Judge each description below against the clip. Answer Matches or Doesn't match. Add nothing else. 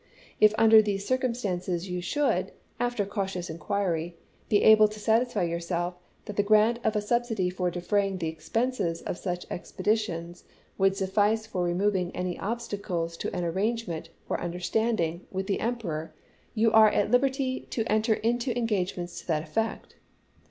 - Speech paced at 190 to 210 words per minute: Doesn't match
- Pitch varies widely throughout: Doesn't match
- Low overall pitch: Doesn't match